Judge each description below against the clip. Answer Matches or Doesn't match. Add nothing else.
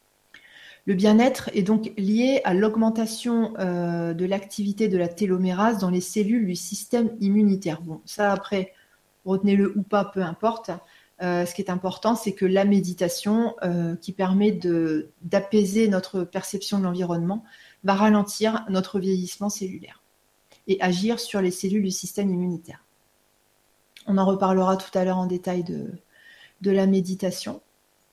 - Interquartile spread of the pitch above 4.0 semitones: Doesn't match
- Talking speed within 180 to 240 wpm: Doesn't match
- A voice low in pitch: Doesn't match